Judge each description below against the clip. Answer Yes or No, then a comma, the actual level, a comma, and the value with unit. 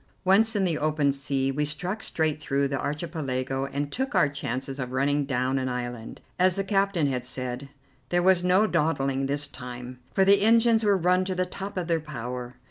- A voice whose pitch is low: No, medium, 145 Hz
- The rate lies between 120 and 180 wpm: No, average, 200 wpm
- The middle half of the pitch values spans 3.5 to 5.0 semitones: No, wide, 5.5 semitones